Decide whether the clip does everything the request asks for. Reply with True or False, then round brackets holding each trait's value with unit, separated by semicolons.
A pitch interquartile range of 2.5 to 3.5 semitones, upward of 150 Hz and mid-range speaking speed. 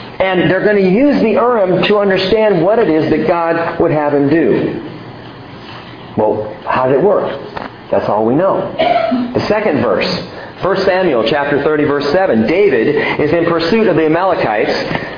False (4.8 semitones; 185 Hz; 170 wpm)